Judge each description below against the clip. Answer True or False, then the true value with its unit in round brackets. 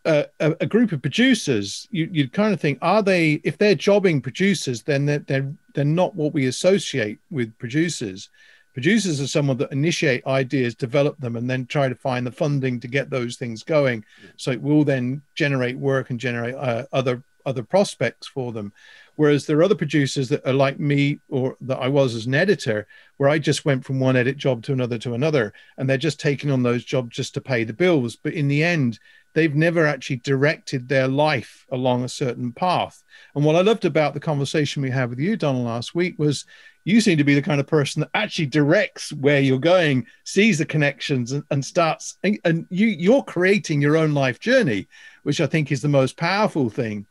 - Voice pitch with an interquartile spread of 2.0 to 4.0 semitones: True (3.6 semitones)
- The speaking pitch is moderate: True (145 Hz)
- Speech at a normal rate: False (210 wpm)